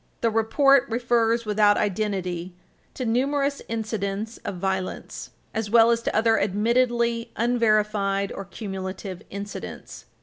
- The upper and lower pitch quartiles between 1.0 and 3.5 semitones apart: Yes, average, 2.9 semitones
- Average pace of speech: No, slow, 115 wpm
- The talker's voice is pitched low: No, high, 220 Hz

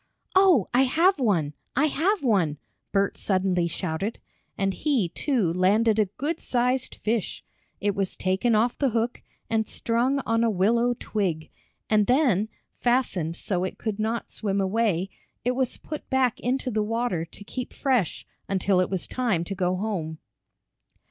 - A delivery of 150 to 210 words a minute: Yes, average, 160 wpm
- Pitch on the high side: Yes, high, 220 Hz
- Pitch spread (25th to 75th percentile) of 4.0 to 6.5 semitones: Yes, average, 4.8 semitones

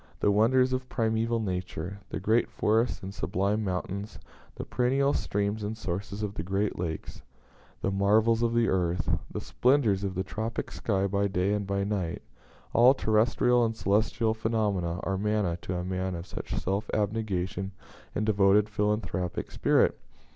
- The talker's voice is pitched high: No, low, 105 Hz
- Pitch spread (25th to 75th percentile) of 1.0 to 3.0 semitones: Yes, average, 2.7 semitones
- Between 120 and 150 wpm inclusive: No, average, 160 wpm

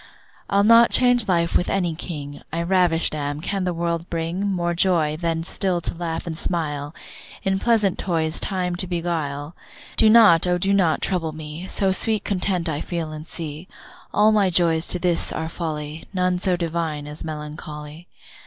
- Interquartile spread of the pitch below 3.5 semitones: Yes, average, 2.8 semitones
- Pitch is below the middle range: No, medium, 170 Hz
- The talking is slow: No, average, 175 wpm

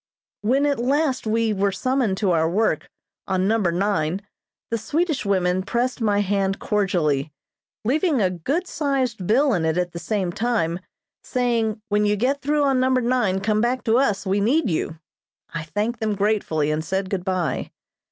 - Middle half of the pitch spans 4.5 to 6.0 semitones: Yes, average, 5.2 semitones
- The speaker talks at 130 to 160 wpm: No, average, 175 wpm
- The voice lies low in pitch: No, high, 210 Hz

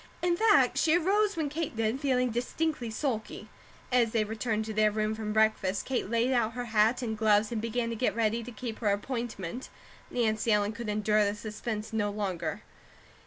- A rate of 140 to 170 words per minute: No, average, 190 wpm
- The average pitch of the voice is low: No, high, 220 Hz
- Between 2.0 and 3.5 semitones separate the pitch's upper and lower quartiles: Yes, narrow, 2.6 semitones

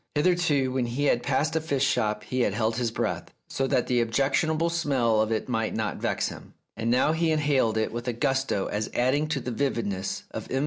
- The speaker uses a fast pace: Yes, fast, 215 wpm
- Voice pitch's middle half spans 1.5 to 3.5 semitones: No, average, 4.2 semitones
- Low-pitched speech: Yes, low, 130 Hz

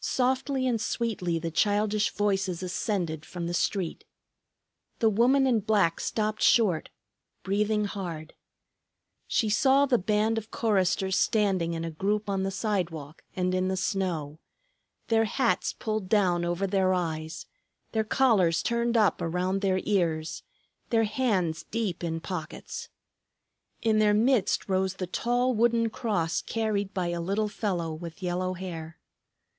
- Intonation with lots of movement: No, average, 4.0 semitones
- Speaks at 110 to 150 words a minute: Yes, average, 140 wpm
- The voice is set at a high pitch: Yes, high, 195 Hz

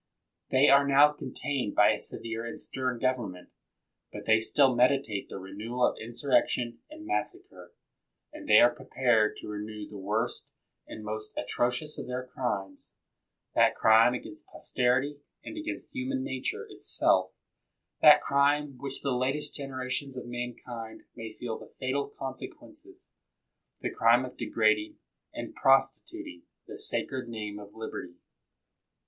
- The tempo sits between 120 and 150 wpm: Yes, average, 145 wpm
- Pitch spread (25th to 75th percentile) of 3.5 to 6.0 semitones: Yes, average, 3.8 semitones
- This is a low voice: Yes, low, 125 Hz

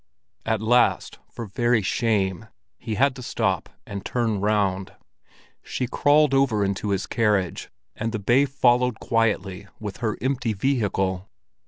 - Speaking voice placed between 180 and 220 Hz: No, low, 110 Hz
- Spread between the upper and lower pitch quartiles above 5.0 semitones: No, average, 3.7 semitones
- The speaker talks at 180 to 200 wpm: No, average, 140 wpm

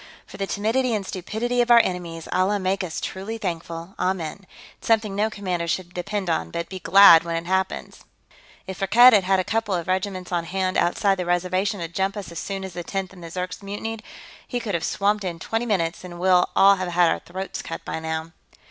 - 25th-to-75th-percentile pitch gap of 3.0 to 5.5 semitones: No, narrow, 2.6 semitones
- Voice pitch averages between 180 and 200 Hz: Yes, high, 190 Hz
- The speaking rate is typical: No, fast, 225 wpm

